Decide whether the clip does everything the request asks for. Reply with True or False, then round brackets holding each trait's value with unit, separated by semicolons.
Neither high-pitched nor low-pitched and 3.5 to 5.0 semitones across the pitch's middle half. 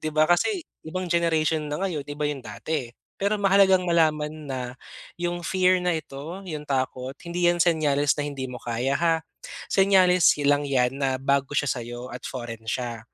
True (150 Hz; 4.6 semitones)